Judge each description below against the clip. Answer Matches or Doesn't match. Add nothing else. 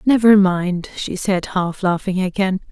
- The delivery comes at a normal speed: Matches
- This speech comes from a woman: Matches